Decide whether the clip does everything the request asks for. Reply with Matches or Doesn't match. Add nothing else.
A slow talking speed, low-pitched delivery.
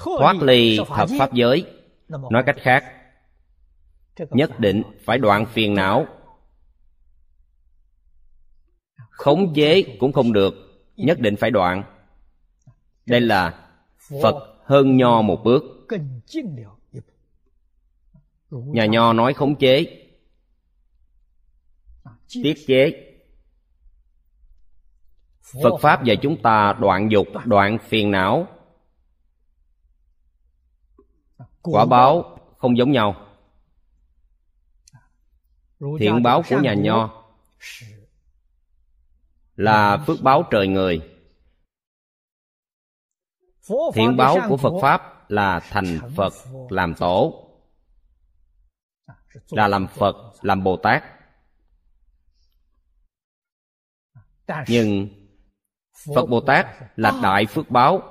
Matches